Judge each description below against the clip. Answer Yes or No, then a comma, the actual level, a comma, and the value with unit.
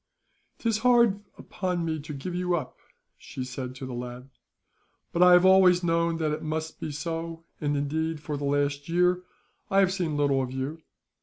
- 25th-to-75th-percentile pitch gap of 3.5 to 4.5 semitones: Yes, average, 3.9 semitones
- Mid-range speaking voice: Yes, medium, 160 Hz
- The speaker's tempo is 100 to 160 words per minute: No, average, 185 wpm